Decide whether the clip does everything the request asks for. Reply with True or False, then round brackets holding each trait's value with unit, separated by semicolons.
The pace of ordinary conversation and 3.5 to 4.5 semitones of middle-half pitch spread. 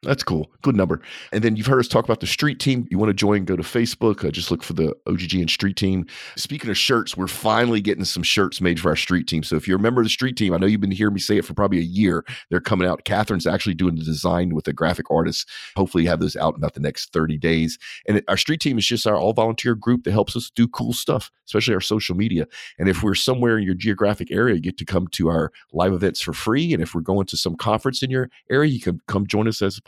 False (285 wpm; 4.1 semitones)